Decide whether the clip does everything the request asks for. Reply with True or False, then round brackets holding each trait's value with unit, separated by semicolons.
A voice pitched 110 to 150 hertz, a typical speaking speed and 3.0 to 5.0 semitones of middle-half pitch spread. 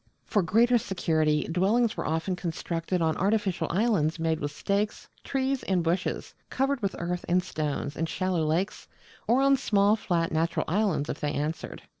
False (180 Hz; 165 wpm; 4.5 semitones)